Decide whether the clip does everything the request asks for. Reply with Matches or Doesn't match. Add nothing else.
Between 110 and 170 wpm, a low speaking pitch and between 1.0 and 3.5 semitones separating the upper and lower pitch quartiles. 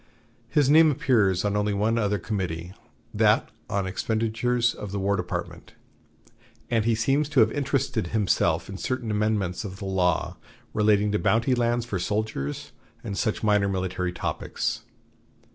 Matches